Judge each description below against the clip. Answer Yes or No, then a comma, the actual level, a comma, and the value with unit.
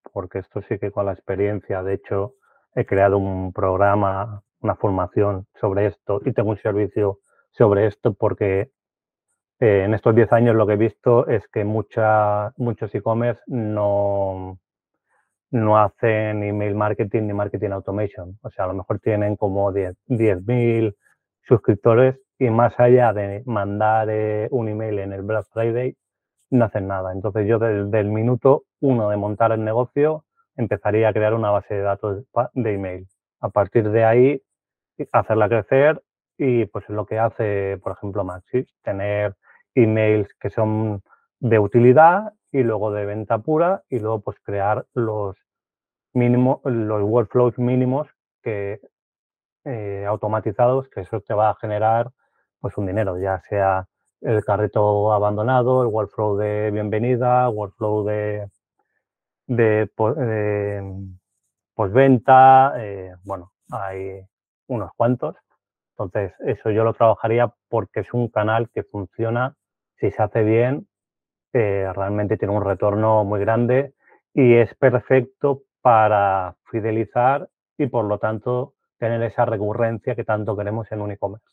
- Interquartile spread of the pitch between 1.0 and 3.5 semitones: Yes, average, 2.9 semitones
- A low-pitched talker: Yes, low, 110 Hz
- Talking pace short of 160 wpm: Yes, average, 145 wpm